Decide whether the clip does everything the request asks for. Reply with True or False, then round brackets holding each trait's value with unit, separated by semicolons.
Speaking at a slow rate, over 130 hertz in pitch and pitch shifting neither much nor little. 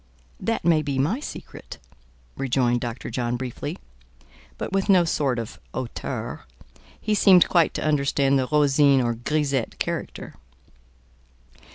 True (130 wpm; 140 Hz; 4.1 semitones)